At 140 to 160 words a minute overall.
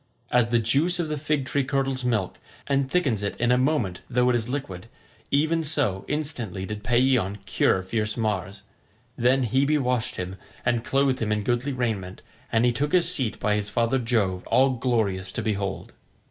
No: average, 185 wpm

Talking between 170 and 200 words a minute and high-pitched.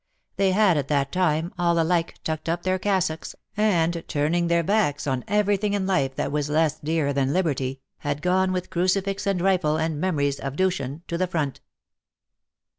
No: average, 180 wpm; medium, 170 Hz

